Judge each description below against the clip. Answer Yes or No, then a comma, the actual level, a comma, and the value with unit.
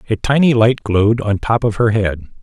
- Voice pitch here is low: Yes, low, 110 Hz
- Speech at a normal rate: No, fast, 220 wpm